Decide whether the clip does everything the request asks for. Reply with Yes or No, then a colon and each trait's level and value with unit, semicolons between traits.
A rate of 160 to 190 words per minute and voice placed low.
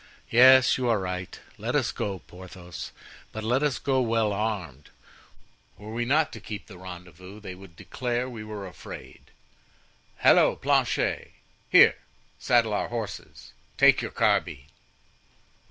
No: average, 140 wpm; low, 105 Hz